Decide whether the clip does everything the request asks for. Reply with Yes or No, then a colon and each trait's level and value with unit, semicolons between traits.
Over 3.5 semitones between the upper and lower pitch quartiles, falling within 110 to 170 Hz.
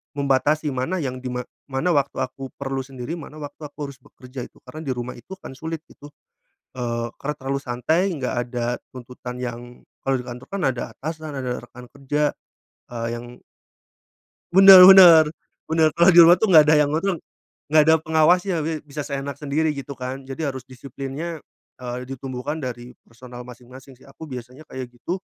Yes: average, 3.9 semitones; low, 135 Hz